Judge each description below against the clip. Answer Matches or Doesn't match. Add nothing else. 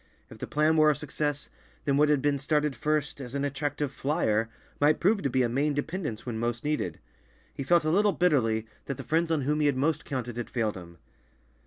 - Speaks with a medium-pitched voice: Matches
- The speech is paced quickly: Matches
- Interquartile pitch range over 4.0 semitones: Doesn't match